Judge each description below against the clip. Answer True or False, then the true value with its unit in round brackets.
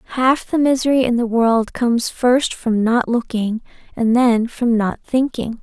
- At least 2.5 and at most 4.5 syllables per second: True (4.3 syllables/s)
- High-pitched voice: True (240 Hz)